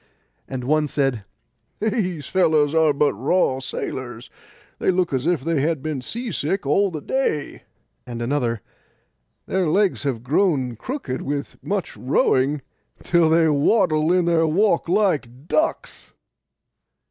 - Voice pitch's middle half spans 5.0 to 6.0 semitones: Yes, average, 5.3 semitones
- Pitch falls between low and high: Yes, medium, 155 Hz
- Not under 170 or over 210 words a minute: No, slow, 135 wpm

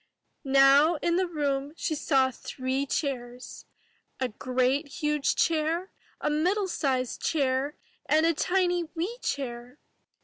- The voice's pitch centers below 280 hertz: No, very high, 285 Hz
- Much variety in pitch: No, average, 4.0 semitones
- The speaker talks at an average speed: No, slow, 130 wpm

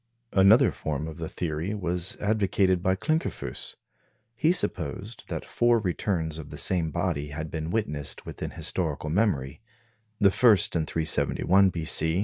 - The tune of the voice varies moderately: Yes, average, 4.2 semitones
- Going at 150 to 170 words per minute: No, average, 140 wpm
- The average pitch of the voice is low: Yes, very low, 90 Hz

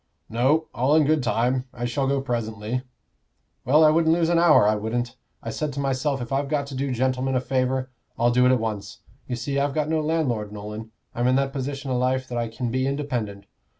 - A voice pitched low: Yes, low, 130 Hz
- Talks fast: Yes, fast, 225 wpm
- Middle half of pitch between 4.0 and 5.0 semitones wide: No, average, 2.9 semitones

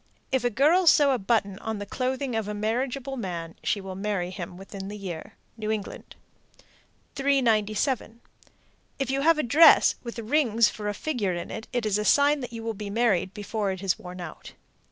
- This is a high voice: Yes, high, 220 Hz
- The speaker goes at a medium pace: Yes, average, 195 wpm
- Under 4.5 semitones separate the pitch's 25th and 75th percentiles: No, average, 4.8 semitones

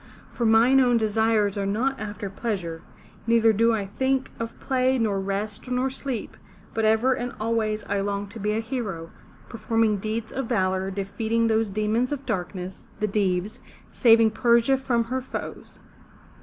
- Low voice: No, high, 220 Hz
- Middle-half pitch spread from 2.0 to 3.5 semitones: Yes, average, 2.7 semitones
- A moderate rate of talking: Yes, average, 165 wpm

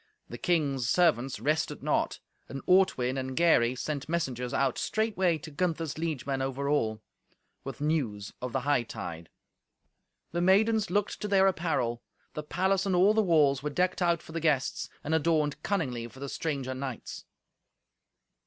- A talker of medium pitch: Yes, medium, 150 Hz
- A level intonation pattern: No, average, 4.9 semitones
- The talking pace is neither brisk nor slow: Yes, average, 155 wpm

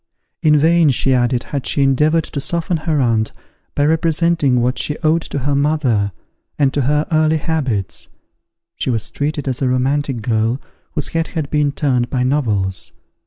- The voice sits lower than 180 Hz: Yes, medium, 140 Hz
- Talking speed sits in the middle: Yes, average, 170 wpm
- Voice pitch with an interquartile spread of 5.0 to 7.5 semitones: No, average, 3.7 semitones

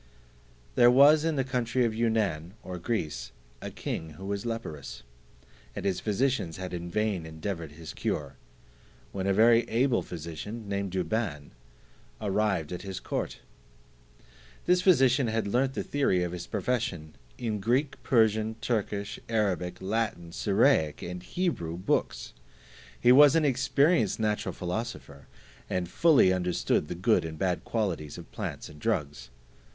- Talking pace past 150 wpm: No, average, 145 wpm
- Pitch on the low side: Yes, low, 100 Hz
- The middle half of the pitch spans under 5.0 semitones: No, wide, 5.4 semitones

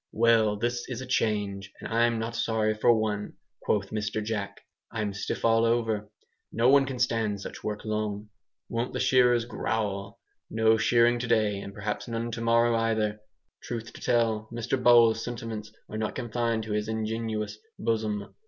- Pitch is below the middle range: Yes, low, 110 Hz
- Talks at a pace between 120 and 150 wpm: No, average, 165 wpm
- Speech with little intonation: Yes, narrow, 1.6 semitones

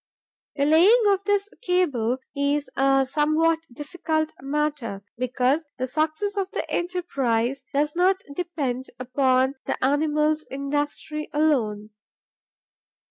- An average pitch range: Yes, average, 3.6 semitones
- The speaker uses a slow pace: Yes, slow, 110 wpm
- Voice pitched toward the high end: Yes, very high, 295 Hz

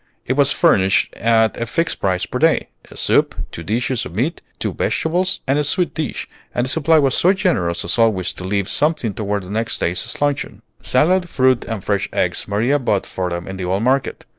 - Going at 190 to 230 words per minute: Yes, fast, 205 wpm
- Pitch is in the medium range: No, low, 115 Hz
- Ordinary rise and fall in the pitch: No, wide, 6.9 semitones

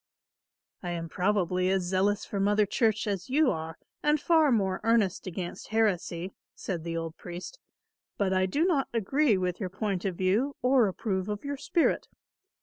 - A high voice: Yes, high, 195 Hz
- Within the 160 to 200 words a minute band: Yes, average, 170 wpm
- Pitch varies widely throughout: No, average, 4.1 semitones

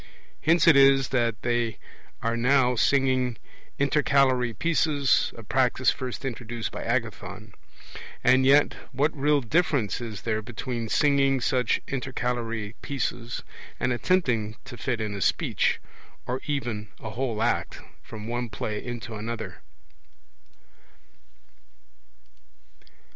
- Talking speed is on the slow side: Yes, slow, 115 wpm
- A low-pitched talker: Yes, low, 125 Hz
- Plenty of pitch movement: No, average, 3.0 semitones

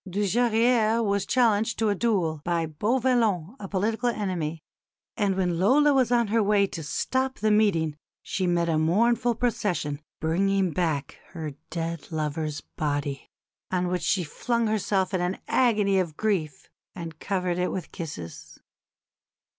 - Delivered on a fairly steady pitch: No, average, 5.0 semitones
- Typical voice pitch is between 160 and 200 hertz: Yes, high, 190 Hz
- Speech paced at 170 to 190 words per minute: No, average, 145 wpm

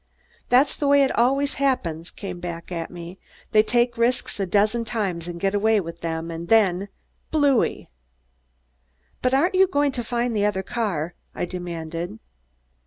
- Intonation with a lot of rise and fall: Yes, wide, 6.0 semitones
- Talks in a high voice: Yes, high, 205 Hz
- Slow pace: No, average, 170 wpm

